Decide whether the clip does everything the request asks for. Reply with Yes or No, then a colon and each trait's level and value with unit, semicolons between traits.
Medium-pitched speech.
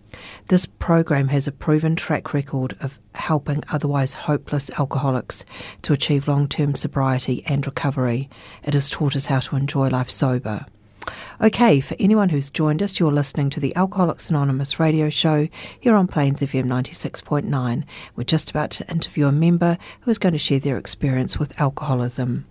Yes: medium, 145 Hz